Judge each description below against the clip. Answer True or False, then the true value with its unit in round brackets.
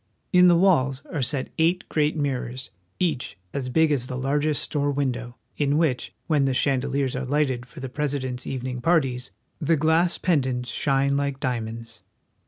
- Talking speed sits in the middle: True (170 wpm)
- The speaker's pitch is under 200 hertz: True (140 Hz)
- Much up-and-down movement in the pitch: False (3.0 semitones)